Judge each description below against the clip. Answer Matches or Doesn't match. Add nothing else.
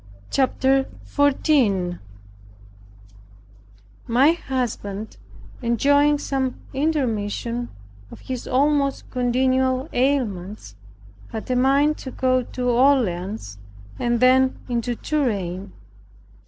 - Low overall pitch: Doesn't match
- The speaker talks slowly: Matches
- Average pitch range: Matches